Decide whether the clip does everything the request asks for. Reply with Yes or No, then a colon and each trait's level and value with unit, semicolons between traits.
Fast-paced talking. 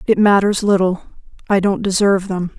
No: average, 160 wpm